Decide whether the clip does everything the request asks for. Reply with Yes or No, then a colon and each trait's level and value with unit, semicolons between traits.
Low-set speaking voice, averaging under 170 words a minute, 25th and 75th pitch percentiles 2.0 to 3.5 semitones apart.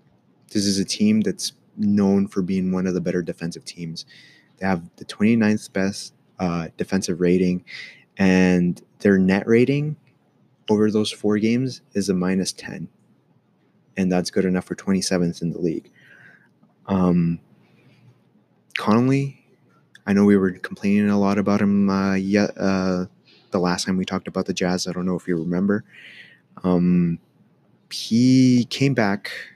Yes: very low, 95 Hz; average, 150 wpm; narrow, 2.4 semitones